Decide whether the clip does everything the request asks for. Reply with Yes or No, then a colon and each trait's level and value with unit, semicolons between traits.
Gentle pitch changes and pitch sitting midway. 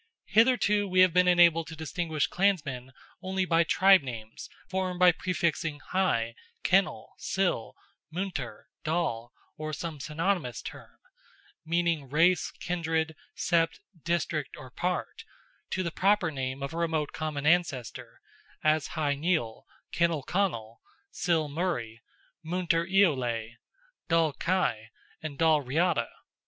No: average, 4.1 semitones; medium, 165 Hz